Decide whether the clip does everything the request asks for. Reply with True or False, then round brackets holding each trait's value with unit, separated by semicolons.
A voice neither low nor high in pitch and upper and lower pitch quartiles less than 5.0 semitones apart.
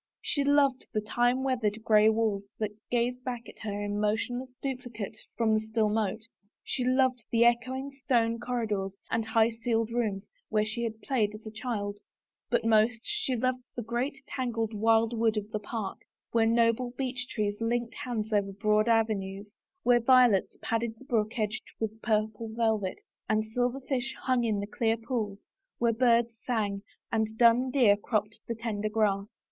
False (225 Hz; 2.4 semitones)